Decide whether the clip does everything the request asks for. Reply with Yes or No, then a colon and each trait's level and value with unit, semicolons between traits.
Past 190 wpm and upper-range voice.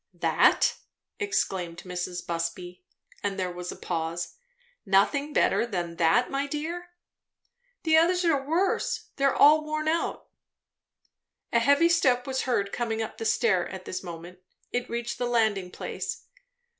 No: average, 145 wpm; high, 230 Hz